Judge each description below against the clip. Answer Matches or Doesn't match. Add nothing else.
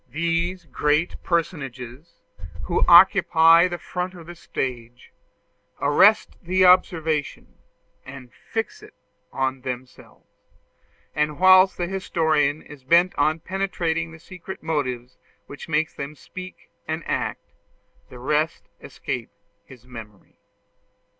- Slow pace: Matches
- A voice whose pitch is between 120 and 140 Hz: Doesn't match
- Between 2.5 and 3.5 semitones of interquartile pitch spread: Doesn't match